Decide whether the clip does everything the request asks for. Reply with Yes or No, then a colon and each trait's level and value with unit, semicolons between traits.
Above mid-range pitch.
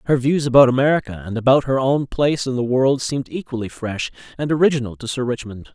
No: low, 130 Hz